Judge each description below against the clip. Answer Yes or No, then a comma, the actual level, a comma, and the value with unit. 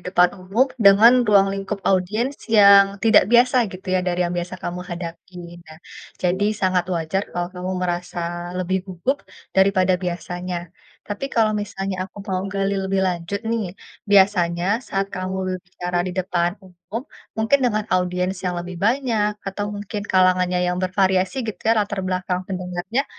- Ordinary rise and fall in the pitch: No, narrow, 2.3 semitones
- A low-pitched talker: No, medium, 185 Hz